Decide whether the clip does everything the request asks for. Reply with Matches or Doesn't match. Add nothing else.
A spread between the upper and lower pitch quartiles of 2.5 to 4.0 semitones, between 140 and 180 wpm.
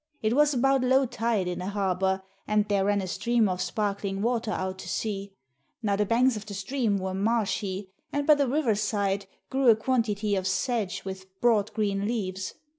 Doesn't match